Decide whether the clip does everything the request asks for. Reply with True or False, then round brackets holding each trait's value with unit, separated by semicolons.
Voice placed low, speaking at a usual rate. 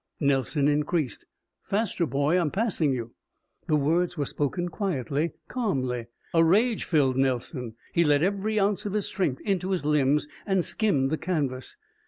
False (155 Hz; 155 wpm)